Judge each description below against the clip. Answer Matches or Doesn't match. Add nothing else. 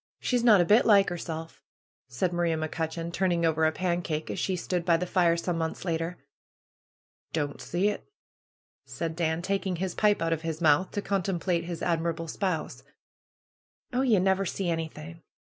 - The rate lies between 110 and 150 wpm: Doesn't match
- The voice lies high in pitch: Doesn't match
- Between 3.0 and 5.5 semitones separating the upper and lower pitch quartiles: Doesn't match